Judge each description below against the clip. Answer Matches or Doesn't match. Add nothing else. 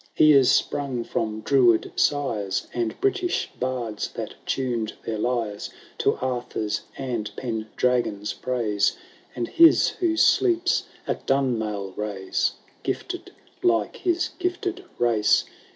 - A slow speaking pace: Matches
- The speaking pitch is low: Matches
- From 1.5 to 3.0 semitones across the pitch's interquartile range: Doesn't match